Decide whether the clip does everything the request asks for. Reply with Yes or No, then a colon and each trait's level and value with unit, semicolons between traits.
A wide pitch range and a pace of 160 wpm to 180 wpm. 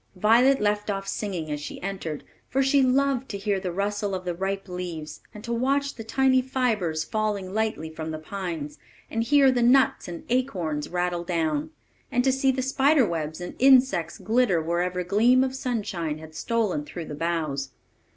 No: wide, 6.8 semitones; average, 190 wpm